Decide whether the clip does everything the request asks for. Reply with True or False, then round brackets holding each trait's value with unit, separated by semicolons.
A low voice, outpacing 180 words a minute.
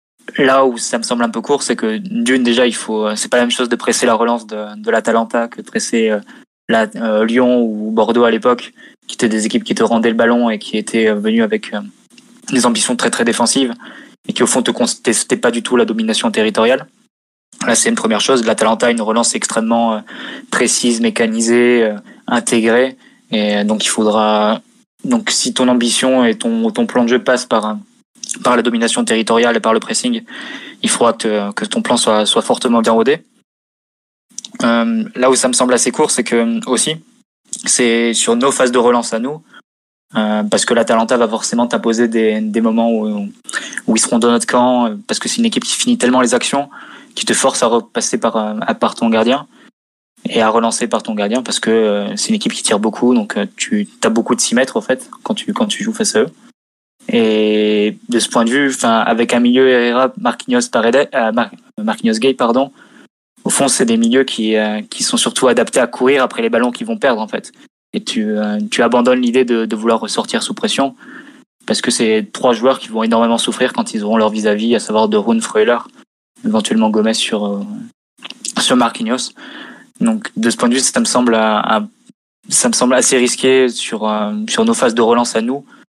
True (120 Hz; 215 wpm)